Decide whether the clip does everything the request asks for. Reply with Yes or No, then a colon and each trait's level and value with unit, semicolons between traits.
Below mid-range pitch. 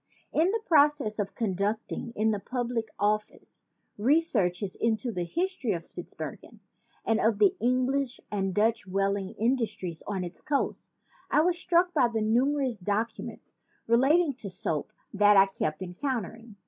No: high, 225 Hz